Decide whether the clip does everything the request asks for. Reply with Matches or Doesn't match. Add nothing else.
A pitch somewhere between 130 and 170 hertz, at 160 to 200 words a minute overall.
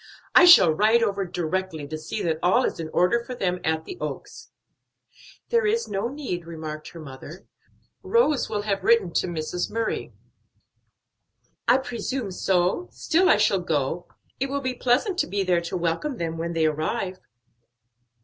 Doesn't match